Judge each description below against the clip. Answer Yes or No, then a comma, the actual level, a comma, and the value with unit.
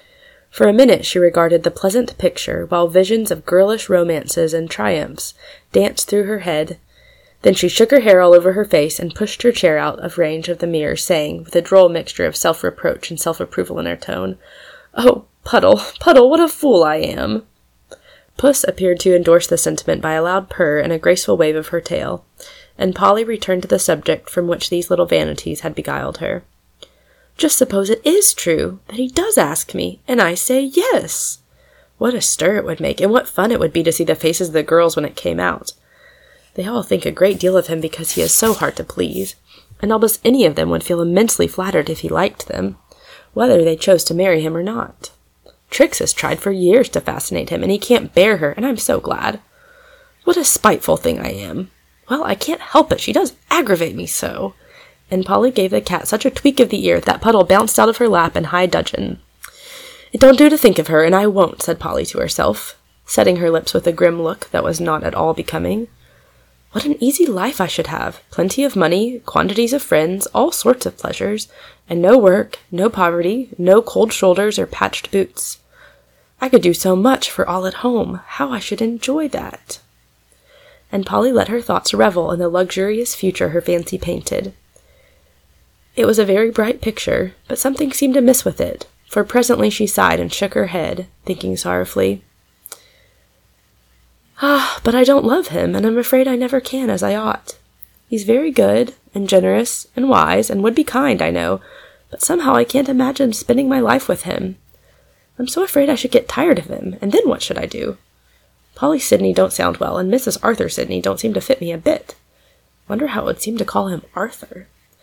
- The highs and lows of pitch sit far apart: Yes, wide, 7.3 semitones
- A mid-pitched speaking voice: No, high, 200 Hz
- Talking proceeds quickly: Yes, fast, 210 wpm